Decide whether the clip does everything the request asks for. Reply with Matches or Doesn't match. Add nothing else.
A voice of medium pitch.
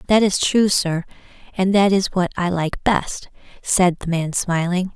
Matches